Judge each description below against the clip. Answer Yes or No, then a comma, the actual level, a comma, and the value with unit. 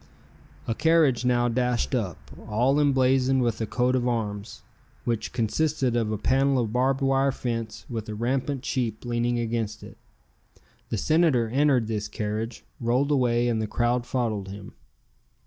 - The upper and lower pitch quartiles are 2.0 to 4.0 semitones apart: Yes, average, 2.8 semitones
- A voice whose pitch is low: Yes, low, 120 Hz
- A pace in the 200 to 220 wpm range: No, average, 155 wpm